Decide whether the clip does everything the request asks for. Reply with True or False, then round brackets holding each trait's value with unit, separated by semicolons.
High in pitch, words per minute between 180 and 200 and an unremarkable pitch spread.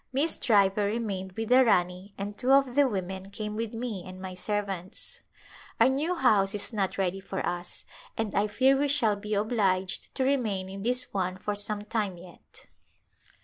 True (205 Hz; 185 wpm; 3.8 semitones)